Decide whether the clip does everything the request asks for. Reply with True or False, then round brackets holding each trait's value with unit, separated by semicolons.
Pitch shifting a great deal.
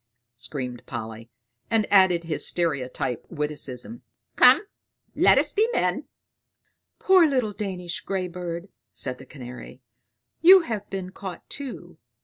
True (7.8 semitones)